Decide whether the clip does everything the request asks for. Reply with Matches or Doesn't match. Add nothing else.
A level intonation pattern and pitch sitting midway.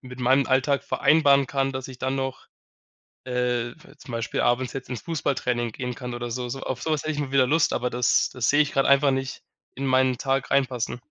Doesn't match